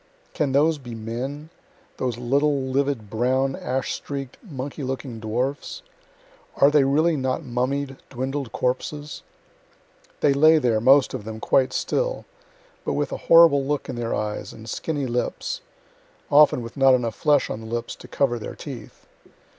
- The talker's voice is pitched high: No, low, 135 Hz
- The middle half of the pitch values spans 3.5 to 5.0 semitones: No, average, 3.1 semitones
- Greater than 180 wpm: No, average, 155 wpm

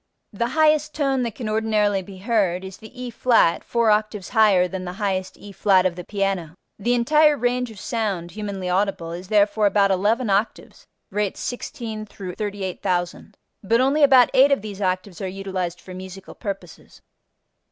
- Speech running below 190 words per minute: Yes, average, 165 wpm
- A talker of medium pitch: No, high, 205 Hz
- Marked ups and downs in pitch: No, average, 3.8 semitones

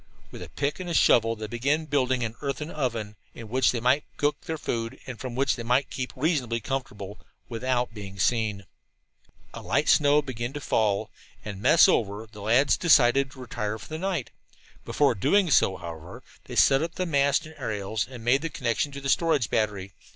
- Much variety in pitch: No, average, 4.5 semitones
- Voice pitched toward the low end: Yes, low, 125 Hz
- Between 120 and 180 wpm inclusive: No, average, 190 wpm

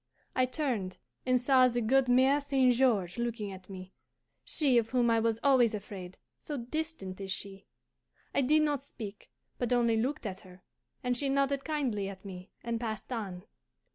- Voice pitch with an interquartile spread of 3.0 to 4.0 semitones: No, average, 5.0 semitones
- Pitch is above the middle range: Yes, high, 235 Hz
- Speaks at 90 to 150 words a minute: No, average, 175 wpm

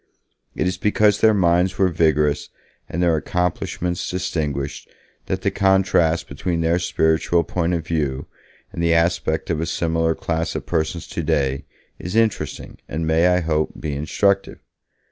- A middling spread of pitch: No, narrow, 2.2 semitones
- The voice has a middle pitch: No, very low, 85 Hz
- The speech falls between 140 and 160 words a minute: Yes, average, 150 wpm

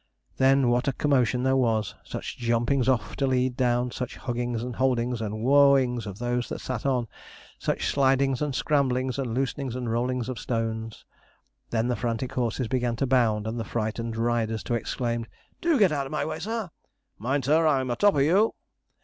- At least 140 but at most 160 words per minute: No, average, 190 wpm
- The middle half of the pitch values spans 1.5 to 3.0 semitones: Yes, narrow, 2.5 semitones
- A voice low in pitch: Yes, low, 125 Hz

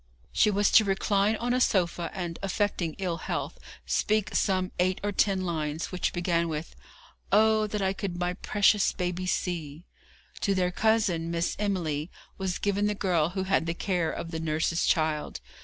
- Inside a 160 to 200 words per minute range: Yes, average, 175 wpm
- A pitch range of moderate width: Yes, average, 3.2 semitones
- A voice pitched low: No, medium, 185 Hz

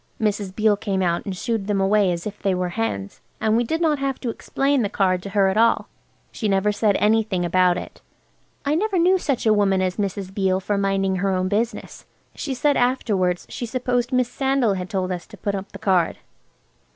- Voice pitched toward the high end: Yes, high, 205 Hz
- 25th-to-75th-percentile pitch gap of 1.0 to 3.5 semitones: No, average, 4.0 semitones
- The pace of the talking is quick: Yes, fast, 220 wpm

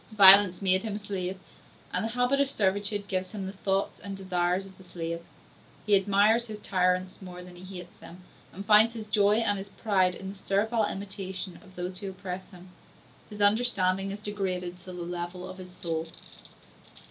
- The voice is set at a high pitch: Yes, high, 195 Hz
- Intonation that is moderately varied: No, narrow, 2.1 semitones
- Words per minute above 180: Yes, average, 190 wpm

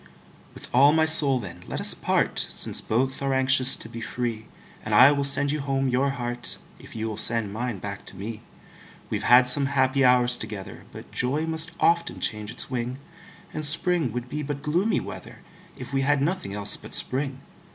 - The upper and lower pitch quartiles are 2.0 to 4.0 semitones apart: Yes, average, 3.4 semitones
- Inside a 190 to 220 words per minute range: Yes, average, 195 wpm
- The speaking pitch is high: No, low, 130 Hz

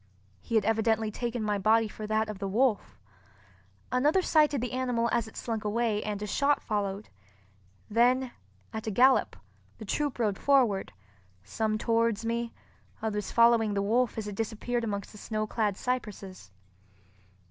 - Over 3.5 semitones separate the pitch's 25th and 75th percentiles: No, narrow, 2.4 semitones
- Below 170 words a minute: Yes, average, 155 wpm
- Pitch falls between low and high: No, high, 220 Hz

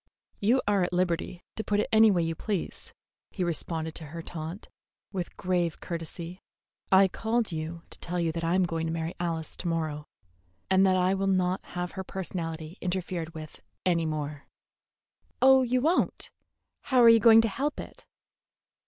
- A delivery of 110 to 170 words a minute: No, average, 180 wpm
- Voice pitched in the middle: Yes, medium, 180 Hz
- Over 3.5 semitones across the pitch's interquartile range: No, average, 3.2 semitones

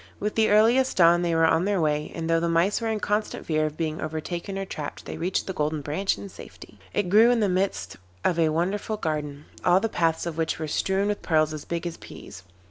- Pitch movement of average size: Yes, average, 4.2 semitones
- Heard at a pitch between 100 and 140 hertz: No, medium, 170 Hz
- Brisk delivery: Yes, fast, 240 wpm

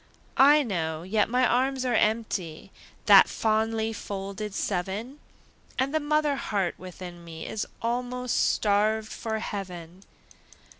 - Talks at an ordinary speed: No, slow, 120 wpm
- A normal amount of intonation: Yes, average, 4.6 semitones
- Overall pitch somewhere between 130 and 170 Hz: No, high, 215 Hz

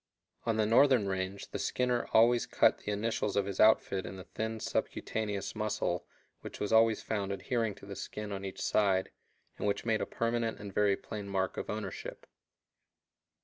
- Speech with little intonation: Yes, narrow, 2.3 semitones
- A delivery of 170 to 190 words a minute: Yes, average, 180 wpm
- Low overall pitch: Yes, low, 105 Hz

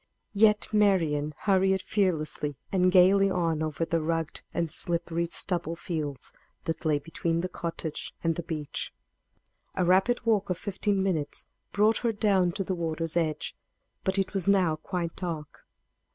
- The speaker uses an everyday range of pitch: Yes, average, 3.2 semitones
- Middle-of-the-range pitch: Yes, medium, 175 Hz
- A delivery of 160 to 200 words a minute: No, average, 150 wpm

